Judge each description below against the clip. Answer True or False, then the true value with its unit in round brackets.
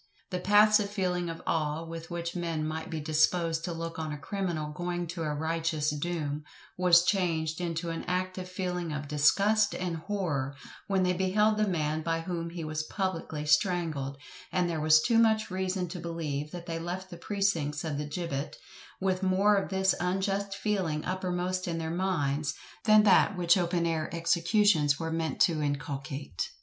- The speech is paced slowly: False (175 wpm)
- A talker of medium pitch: True (170 Hz)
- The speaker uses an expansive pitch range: False (3.0 semitones)